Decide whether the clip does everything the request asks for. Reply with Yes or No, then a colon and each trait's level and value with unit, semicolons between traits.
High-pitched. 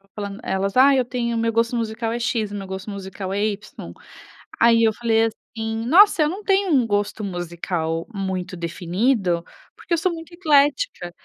Yes: high, 220 Hz